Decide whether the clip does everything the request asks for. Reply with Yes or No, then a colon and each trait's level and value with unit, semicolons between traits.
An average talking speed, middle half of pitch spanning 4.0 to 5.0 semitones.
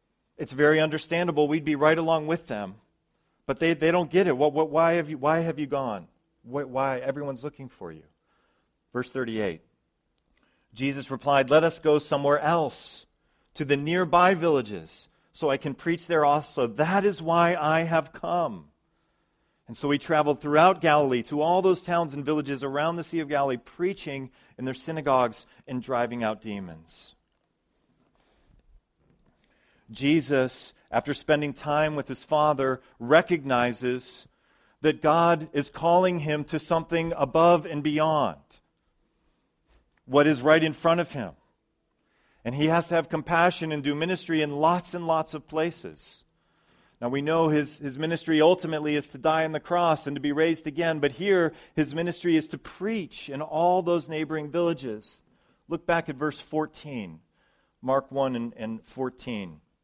No: average, 160 wpm; average, 3.3 semitones